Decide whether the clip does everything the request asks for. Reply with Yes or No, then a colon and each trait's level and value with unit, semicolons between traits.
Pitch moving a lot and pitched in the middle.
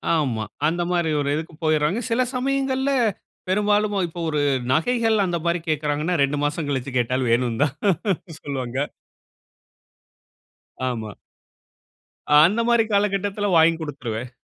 Yes: wide, 6.6 semitones; medium, 160 Hz